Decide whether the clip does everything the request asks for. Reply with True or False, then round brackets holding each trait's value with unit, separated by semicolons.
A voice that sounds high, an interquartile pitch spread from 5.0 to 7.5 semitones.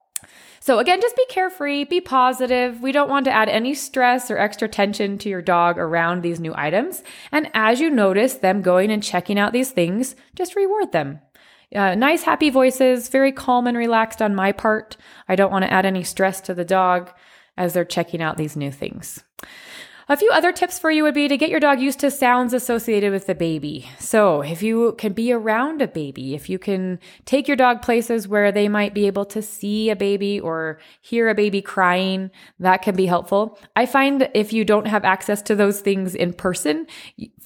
True (210 Hz; 5.6 semitones)